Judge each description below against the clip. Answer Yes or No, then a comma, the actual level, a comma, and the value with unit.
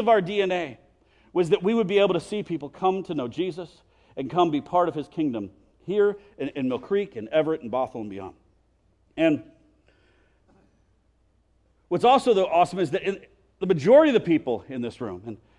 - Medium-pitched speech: Yes, medium, 180 Hz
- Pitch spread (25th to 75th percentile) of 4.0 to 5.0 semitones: Yes, average, 4.7 semitones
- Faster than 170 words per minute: Yes, average, 195 wpm